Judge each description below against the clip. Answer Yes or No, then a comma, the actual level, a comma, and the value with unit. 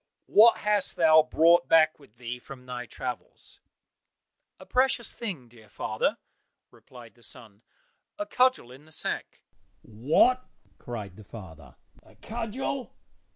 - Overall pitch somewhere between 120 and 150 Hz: Yes, low, 135 Hz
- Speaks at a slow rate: Yes, slow, 130 wpm